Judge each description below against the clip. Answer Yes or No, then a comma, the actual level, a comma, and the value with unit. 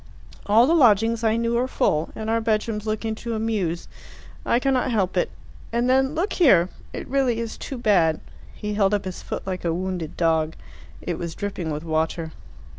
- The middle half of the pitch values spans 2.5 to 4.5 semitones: No, average, 5.0 semitones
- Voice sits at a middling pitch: No, high, 215 Hz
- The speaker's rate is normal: Yes, average, 190 wpm